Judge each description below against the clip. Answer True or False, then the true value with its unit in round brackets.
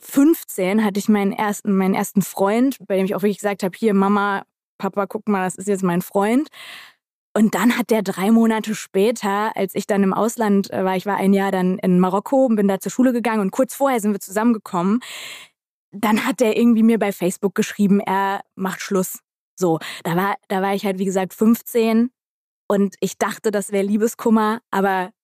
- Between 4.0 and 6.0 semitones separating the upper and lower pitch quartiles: False (2.4 semitones)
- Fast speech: True (200 wpm)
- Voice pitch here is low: False (200 Hz)